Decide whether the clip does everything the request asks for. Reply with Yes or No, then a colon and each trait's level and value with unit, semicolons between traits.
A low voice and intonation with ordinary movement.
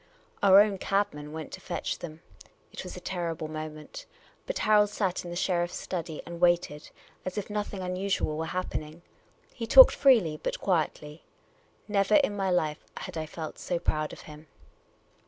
No: medium, 175 Hz; average, 4.1 semitones